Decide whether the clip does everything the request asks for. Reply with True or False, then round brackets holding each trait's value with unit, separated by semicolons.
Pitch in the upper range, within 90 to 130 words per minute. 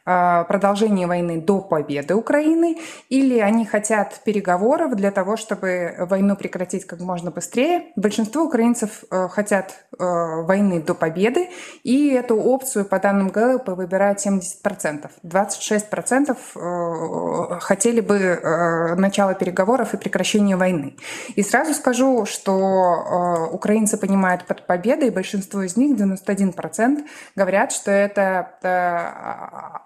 True (200 Hz; 110 wpm)